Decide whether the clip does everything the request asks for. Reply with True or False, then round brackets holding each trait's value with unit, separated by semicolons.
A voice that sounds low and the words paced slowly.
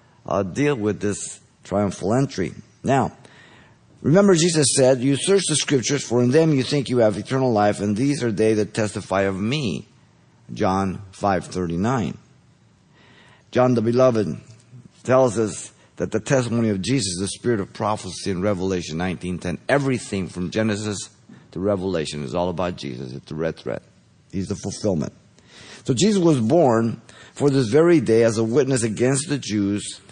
False (110 Hz; 160 wpm)